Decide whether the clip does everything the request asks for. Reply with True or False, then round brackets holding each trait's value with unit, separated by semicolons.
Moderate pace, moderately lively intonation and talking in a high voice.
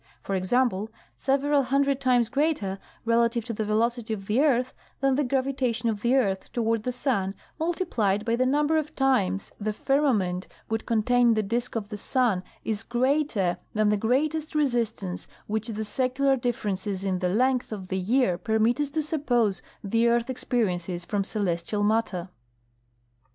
True (160 wpm; 4.2 semitones; 230 Hz)